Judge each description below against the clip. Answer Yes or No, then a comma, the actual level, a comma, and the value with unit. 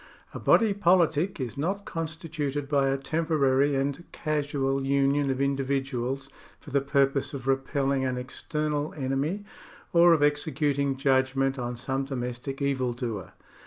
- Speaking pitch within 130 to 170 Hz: Yes, medium, 140 Hz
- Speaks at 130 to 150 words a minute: Yes, slow, 135 wpm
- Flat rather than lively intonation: Yes, narrow, 1.9 semitones